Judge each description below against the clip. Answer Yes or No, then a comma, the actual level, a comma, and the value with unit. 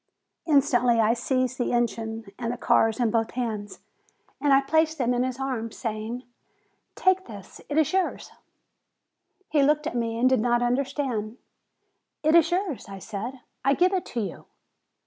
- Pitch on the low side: No, high, 245 Hz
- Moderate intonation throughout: Yes, average, 3.9 semitones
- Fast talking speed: No, average, 165 wpm